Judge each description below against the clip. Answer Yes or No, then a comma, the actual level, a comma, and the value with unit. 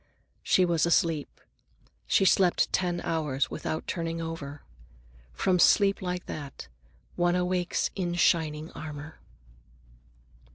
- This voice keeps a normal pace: No, slow, 110 wpm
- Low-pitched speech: No, medium, 165 Hz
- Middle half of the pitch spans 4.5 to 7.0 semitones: No, narrow, 2.5 semitones